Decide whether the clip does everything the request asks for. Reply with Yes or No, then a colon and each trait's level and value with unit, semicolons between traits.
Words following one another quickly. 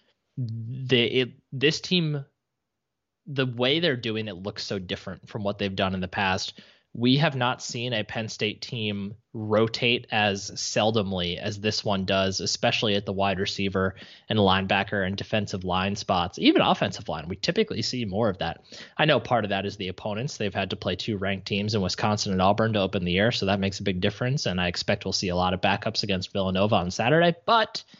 Yes: fast, 210 wpm